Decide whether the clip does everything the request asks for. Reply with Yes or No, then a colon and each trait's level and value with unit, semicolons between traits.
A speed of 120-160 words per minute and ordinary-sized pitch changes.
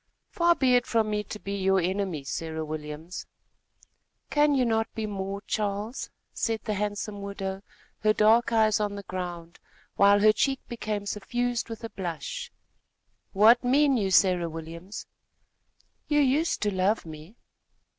Yes: average, 150 wpm; average, 3.4 semitones